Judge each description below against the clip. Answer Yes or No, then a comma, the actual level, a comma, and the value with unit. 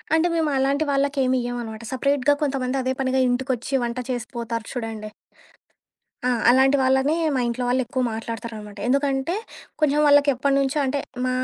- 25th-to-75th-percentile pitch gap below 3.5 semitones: Yes, narrow, 2.5 semitones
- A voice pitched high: Yes, very high, 260 Hz